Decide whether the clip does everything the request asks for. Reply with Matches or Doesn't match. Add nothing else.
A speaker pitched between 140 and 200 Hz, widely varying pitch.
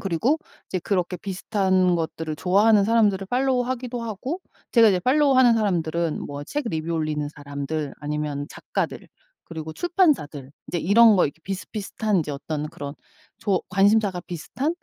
Matches